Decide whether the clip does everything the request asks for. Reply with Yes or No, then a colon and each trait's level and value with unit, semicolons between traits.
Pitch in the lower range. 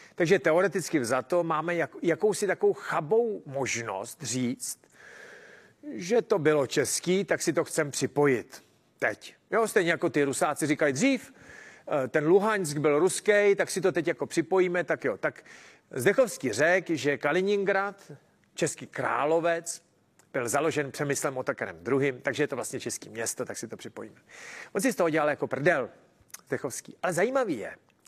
No: medium, 170 Hz